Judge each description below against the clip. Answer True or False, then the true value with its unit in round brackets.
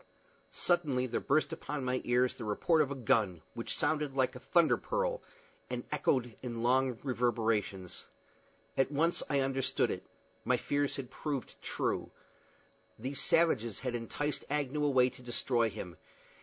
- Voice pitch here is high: False (130 Hz)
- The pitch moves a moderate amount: True (3.5 semitones)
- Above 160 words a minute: False (150 wpm)